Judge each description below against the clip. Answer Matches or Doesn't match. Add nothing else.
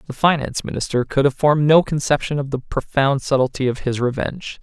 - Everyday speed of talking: Matches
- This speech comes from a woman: Doesn't match